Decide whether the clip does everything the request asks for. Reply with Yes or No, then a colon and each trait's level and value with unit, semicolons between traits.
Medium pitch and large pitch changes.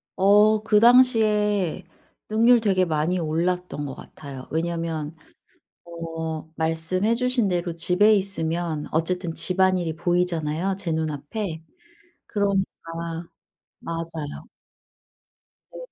No: medium, 175 Hz; average, 3.8 semitones